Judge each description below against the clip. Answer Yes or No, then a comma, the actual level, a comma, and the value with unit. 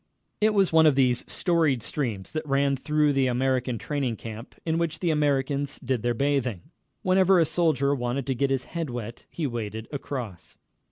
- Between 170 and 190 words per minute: Yes, average, 180 wpm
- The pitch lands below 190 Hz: Yes, medium, 140 Hz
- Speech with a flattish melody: No, average, 4.0 semitones